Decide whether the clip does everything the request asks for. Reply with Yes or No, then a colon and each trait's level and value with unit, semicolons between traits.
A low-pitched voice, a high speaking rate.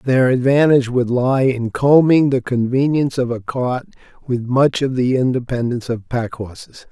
No: low, 125 Hz; average, 165 wpm